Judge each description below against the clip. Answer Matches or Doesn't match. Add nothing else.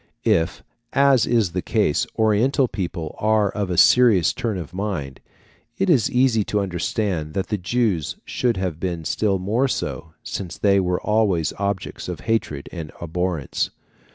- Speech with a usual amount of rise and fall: Matches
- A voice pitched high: Doesn't match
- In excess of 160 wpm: Doesn't match